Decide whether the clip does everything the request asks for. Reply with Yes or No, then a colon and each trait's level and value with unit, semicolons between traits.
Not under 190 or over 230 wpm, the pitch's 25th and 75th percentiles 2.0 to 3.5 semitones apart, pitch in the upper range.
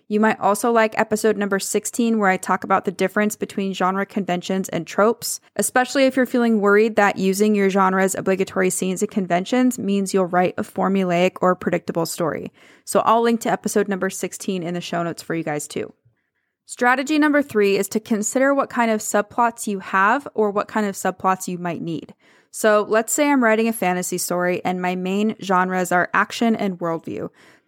Yes: average, 195 wpm; average, 3.0 semitones; high, 200 Hz